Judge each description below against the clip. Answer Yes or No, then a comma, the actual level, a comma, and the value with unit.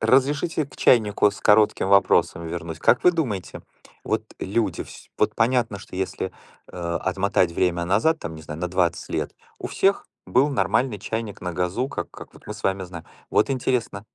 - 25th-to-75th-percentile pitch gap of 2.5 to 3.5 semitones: No, wide, 5.6 semitones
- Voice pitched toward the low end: Yes, low, 100 Hz